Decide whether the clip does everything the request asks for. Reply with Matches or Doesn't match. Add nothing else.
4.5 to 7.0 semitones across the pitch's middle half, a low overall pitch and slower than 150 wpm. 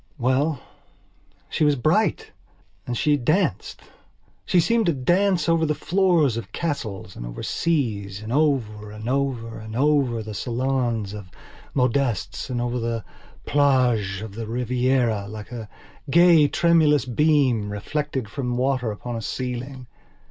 Matches